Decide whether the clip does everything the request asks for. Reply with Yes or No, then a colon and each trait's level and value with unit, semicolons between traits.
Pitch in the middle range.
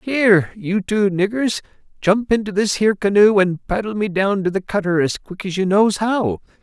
No: high, 200 Hz